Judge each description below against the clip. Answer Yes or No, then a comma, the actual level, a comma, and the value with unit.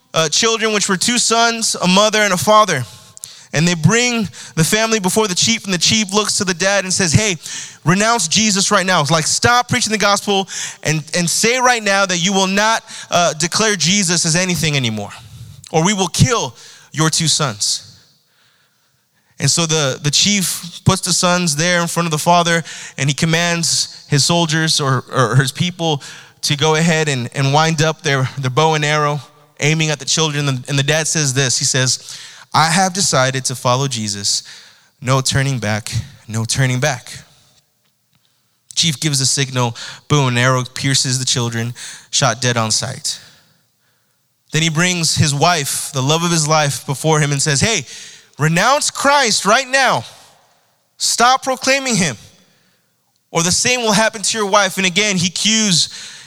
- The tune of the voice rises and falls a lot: Yes, wide, 5.9 semitones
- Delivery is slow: No, average, 180 wpm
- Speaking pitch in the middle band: Yes, medium, 160 Hz